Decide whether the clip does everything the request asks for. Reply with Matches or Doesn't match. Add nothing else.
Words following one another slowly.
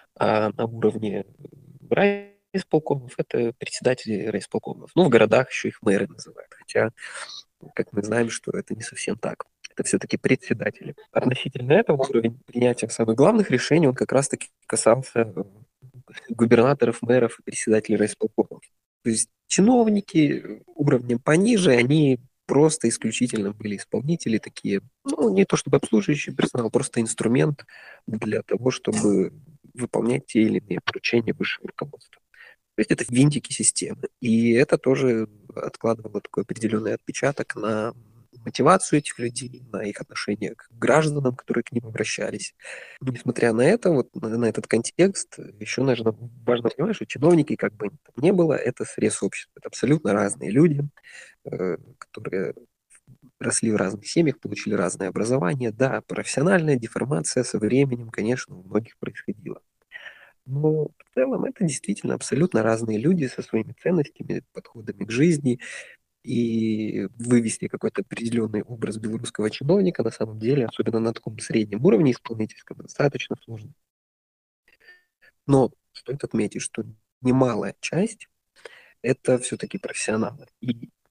Doesn't match